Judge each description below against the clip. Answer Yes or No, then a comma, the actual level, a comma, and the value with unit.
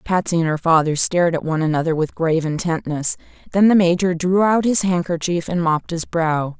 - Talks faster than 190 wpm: Yes, average, 200 wpm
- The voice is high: No, medium, 170 Hz